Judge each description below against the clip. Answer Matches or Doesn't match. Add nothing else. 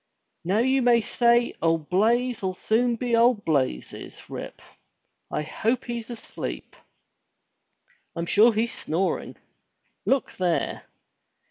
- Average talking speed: Doesn't match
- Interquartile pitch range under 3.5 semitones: Doesn't match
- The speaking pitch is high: Matches